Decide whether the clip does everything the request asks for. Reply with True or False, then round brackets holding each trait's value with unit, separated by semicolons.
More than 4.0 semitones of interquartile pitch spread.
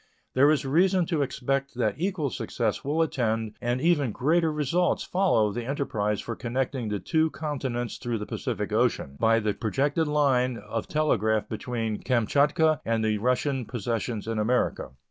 True (4.8 semitones)